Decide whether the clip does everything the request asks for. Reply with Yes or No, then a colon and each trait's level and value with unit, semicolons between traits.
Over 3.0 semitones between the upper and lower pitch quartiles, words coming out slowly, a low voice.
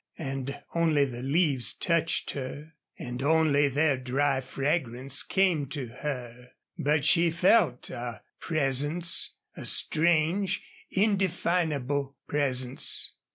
No: average, 4.0 semitones; slow, 105 wpm; medium, 145 Hz